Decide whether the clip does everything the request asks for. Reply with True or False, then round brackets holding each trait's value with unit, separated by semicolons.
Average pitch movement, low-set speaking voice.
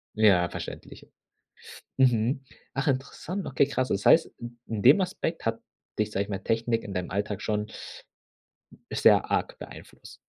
True (4.4 semitones; 115 Hz)